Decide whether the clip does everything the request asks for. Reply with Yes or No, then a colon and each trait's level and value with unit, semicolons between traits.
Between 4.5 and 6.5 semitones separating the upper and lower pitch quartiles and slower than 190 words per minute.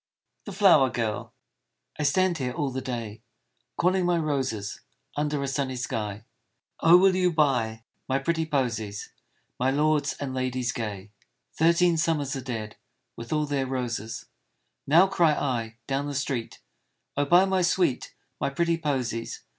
Yes: average, 5.2 semitones; average, 160 wpm